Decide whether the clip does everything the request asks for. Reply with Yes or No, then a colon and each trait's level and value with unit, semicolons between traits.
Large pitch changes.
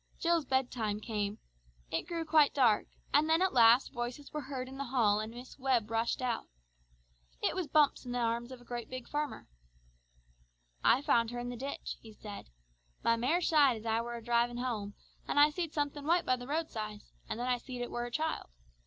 No: average, 3.8 semitones